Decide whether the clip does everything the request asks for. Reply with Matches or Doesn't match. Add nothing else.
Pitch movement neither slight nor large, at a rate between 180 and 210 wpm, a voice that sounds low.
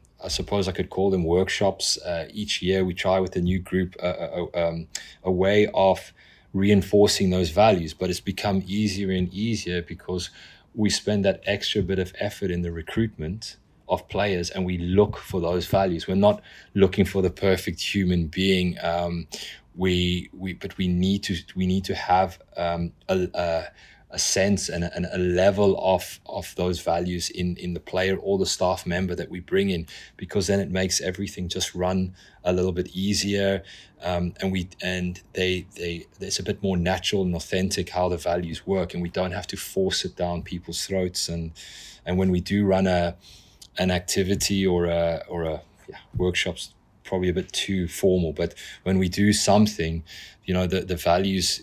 Doesn't match